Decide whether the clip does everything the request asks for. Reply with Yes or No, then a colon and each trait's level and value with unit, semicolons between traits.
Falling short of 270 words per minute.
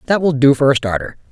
No: fast, 275 wpm